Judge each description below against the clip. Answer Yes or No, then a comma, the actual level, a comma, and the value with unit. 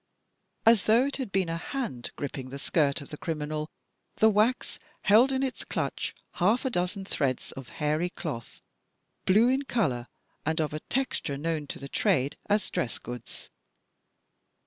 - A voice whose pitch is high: No, medium, 165 Hz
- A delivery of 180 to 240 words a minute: No, average, 170 wpm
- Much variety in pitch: Yes, wide, 7.6 semitones